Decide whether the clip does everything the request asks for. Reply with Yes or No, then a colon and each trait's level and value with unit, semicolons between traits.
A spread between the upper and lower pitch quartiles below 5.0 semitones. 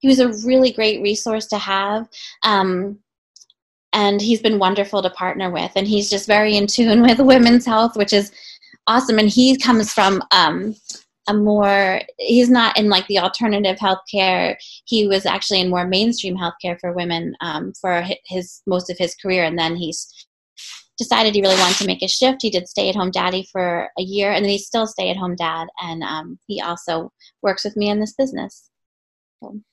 Yes: average, 3.1 semitones